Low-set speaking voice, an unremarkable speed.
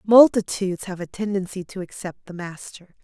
No: high, 190 Hz; average, 160 wpm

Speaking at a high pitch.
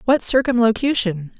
Yes: high, 230 Hz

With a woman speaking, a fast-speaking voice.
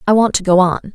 Yes: female; fast, 320 wpm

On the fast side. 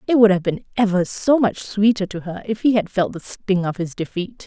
Yes: fast, 255 wpm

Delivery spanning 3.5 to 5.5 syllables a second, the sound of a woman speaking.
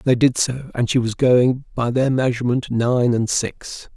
No: 4.5 syllables/s; male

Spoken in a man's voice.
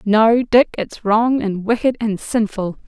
No: female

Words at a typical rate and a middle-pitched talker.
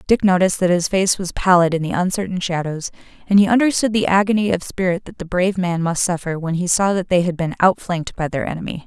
No: fast, 235 wpm; medium, 180 Hz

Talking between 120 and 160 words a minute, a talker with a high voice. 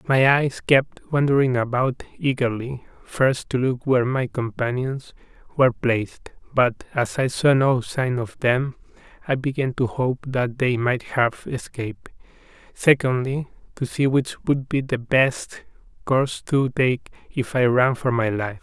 No: average, 155 wpm; low, 130 Hz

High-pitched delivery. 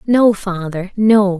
Yes: high, 200 Hz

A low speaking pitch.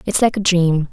No: medium, 185 Hz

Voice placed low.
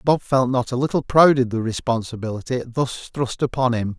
Yes: low, 125 Hz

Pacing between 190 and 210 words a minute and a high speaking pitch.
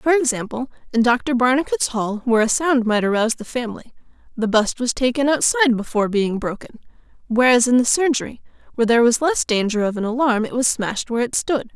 Yes: average, 200 wpm; high, 245 Hz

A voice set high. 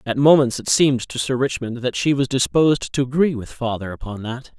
No: low, 130 Hz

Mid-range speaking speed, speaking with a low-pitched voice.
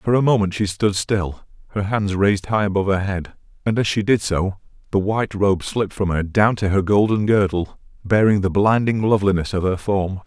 No: fast, 210 wpm; low, 100 Hz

